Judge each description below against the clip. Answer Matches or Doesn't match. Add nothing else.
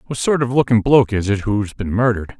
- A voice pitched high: Doesn't match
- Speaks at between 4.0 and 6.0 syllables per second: Doesn't match